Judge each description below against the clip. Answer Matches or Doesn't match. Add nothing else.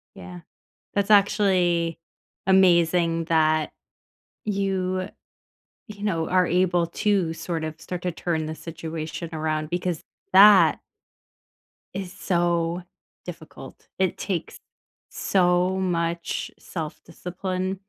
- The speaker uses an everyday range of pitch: Doesn't match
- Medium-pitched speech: Matches